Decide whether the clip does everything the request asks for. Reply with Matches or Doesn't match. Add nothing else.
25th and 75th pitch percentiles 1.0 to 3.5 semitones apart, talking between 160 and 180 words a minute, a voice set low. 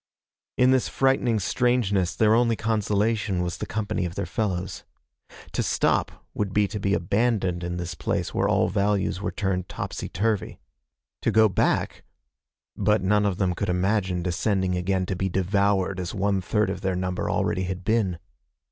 Matches